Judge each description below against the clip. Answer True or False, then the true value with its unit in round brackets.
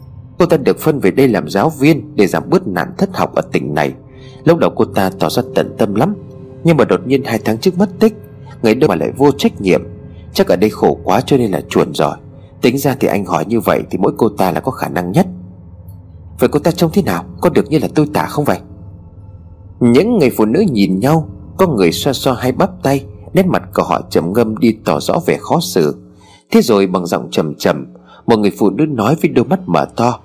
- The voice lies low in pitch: True (125 Hz)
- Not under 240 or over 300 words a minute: True (245 wpm)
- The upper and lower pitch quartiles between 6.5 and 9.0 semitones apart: True (8.2 semitones)